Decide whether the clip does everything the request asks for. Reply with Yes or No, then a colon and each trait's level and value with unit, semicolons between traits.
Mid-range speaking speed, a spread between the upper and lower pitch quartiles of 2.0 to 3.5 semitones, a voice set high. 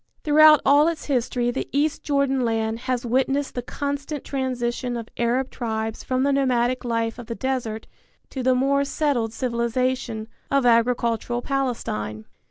Yes: average, 150 wpm; average, 2.8 semitones; very high, 250 Hz